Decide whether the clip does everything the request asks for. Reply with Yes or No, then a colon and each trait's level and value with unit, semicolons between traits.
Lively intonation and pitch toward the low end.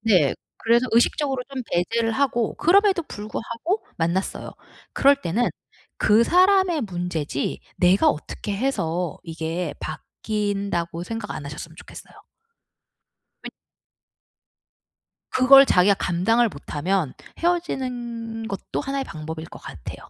No: wide, 6.9 semitones; high, 220 Hz